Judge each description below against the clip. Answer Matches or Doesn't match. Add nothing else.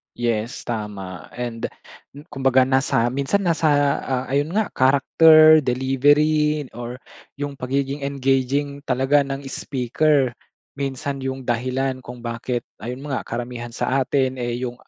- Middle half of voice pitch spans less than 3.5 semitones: Matches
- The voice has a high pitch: Doesn't match